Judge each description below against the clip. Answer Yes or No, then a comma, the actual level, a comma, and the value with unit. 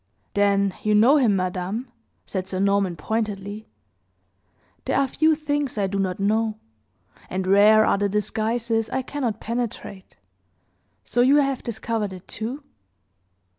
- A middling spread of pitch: Yes, average, 3.4 semitones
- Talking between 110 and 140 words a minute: Yes, slow, 135 wpm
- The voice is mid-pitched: No, high, 215 Hz